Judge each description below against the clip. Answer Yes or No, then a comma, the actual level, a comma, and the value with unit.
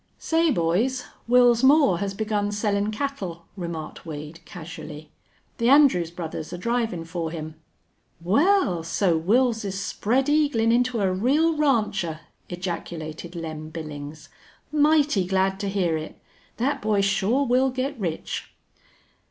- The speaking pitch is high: Yes, high, 200 Hz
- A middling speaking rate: No, slow, 125 wpm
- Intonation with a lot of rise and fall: Yes, wide, 6.9 semitones